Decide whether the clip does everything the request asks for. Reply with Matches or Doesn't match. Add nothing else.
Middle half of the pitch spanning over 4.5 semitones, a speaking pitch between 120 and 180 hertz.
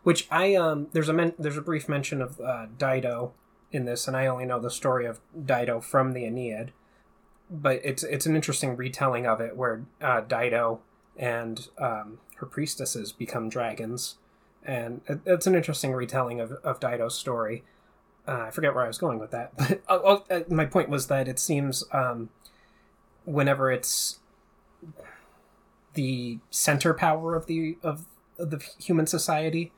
Matches